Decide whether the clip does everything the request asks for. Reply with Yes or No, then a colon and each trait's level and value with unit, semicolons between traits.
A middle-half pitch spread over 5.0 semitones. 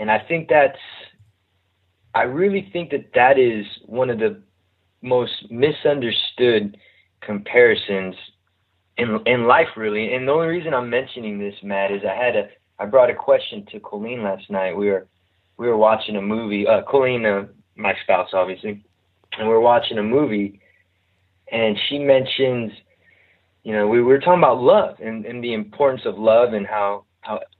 No: average, 4.1 semitones